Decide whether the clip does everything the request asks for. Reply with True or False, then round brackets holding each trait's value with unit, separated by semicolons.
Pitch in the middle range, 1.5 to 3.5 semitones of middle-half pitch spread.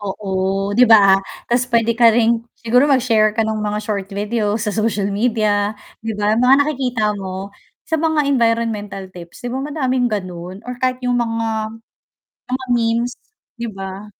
False (225 Hz; 3.0 semitones)